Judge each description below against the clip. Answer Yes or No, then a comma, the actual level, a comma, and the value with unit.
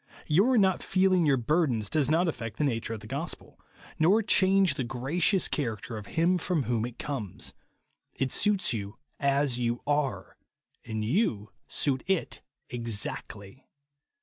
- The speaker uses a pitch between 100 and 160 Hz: Yes, medium, 140 Hz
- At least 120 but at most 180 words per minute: Yes, average, 160 wpm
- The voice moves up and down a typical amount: No, wide, 7.3 semitones